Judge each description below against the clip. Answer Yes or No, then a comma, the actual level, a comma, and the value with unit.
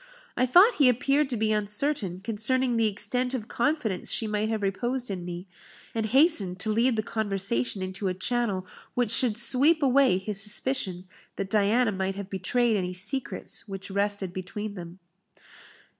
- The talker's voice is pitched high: Yes, high, 215 Hz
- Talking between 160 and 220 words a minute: Yes, average, 165 wpm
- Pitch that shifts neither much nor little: Yes, average, 4.4 semitones